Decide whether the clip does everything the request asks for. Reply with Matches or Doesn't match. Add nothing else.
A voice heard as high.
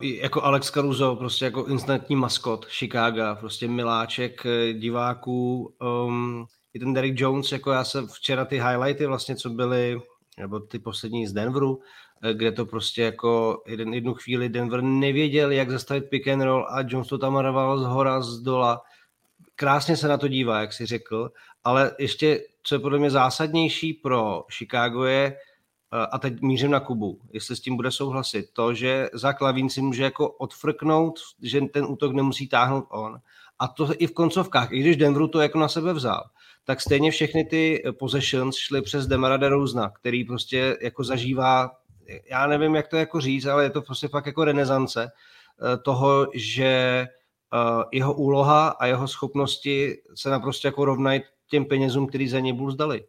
Doesn't match